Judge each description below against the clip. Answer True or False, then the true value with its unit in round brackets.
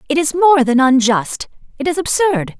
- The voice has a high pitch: True (285 Hz)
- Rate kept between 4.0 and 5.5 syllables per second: True (4.8 syllables/s)